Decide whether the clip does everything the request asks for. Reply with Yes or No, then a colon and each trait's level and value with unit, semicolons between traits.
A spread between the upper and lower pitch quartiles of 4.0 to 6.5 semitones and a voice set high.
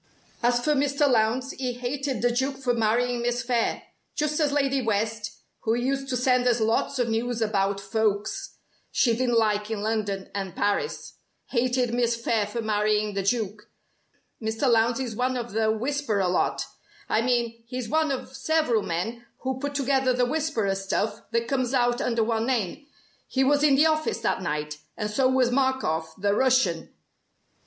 No: average, 3.3 semitones; high, 240 Hz